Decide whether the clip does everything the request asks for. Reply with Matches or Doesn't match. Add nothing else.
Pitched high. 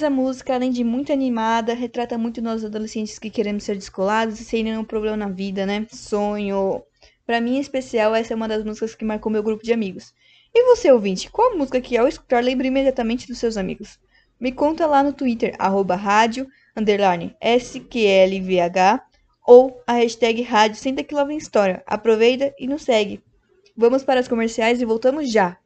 Matches